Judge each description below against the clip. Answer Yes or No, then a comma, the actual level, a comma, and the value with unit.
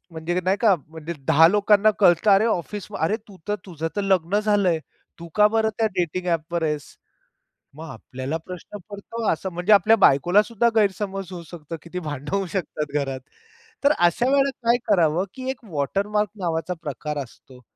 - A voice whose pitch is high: No, medium, 180 Hz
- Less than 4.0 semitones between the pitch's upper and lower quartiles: No, average, 4.4 semitones